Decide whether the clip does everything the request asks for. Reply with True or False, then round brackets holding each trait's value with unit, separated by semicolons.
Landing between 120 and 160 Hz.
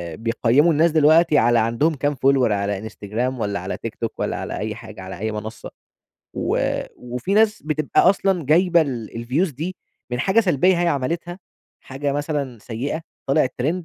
True (140 Hz)